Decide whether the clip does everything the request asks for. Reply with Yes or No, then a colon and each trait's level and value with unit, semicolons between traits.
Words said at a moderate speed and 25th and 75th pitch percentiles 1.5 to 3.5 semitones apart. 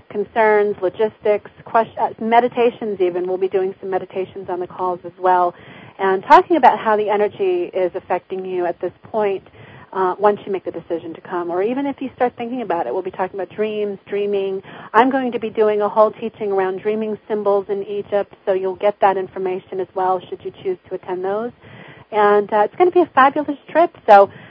No: fast, 210 wpm; average, 2.8 semitones